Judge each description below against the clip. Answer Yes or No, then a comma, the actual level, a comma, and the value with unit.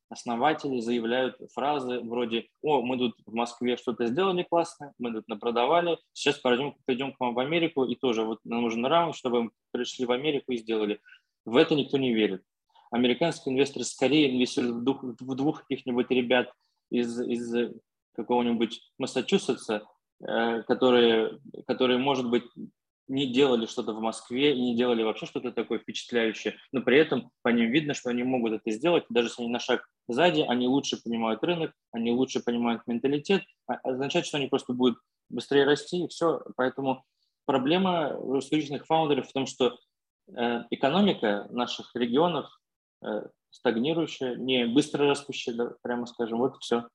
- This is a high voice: No, low, 125 Hz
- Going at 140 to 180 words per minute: Yes, average, 155 wpm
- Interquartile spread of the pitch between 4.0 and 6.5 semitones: No, average, 3.0 semitones